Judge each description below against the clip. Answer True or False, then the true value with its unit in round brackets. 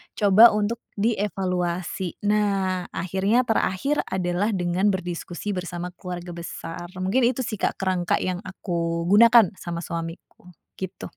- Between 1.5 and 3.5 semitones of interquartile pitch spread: True (2.9 semitones)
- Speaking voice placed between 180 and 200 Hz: True (185 Hz)